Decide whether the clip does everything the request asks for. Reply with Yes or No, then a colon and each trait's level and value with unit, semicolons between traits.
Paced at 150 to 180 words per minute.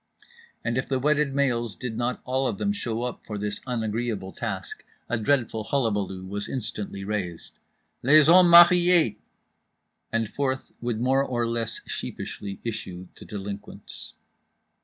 No: average, 140 wpm